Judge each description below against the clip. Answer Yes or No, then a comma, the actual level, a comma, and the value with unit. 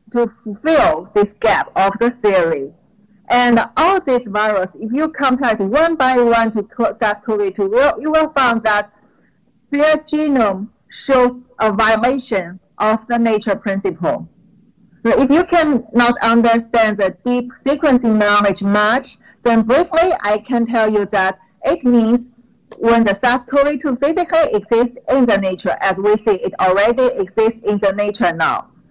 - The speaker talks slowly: No, average, 150 wpm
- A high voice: Yes, high, 230 Hz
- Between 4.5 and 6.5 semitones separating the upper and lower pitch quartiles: No, average, 3.9 semitones